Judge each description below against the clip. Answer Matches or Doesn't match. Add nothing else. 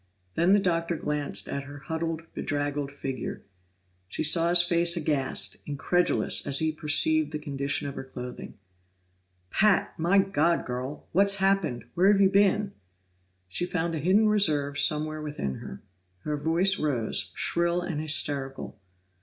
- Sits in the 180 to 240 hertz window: Doesn't match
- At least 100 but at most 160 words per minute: Matches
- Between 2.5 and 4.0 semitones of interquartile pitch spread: Matches